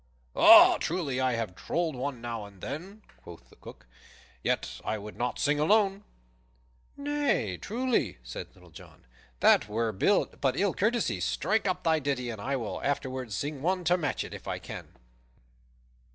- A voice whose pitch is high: No, medium, 140 Hz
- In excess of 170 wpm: No, average, 160 wpm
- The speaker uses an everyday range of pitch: No, wide, 8.3 semitones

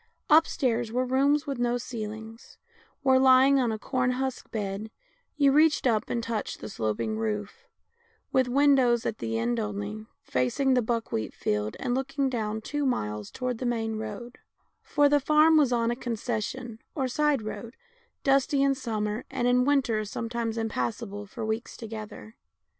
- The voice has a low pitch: No, high, 235 Hz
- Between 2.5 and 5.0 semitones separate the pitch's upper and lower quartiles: Yes, average, 3.5 semitones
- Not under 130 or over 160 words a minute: No, average, 170 wpm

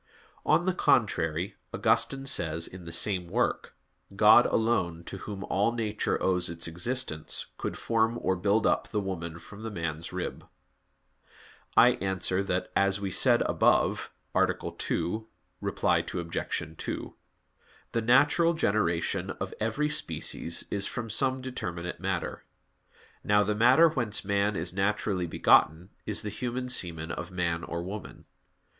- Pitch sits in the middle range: No, low, 100 Hz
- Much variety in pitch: No, average, 4.7 semitones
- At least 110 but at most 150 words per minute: Yes, average, 140 wpm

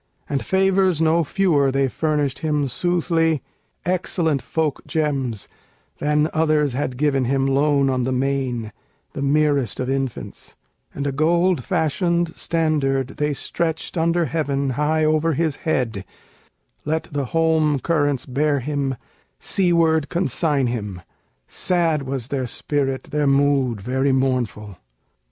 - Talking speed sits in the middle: No, slow, 130 wpm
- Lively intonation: No, average, 3.2 semitones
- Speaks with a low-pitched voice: No, medium, 145 Hz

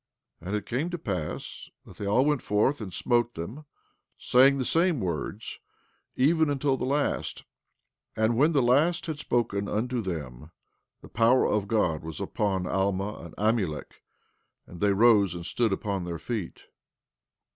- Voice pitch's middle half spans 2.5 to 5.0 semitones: No, wide, 5.6 semitones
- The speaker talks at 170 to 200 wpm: No, average, 160 wpm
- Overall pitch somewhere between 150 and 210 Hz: No, low, 110 Hz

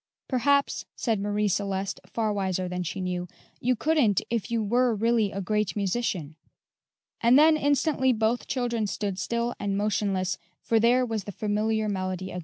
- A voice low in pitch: No, high, 215 Hz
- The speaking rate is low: No, average, 165 wpm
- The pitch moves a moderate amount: Yes, average, 3.5 semitones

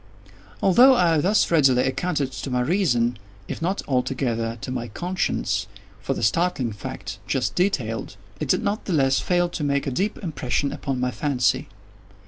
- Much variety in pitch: Yes, wide, 6.0 semitones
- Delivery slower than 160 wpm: No, average, 165 wpm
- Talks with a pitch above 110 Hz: Yes, low, 135 Hz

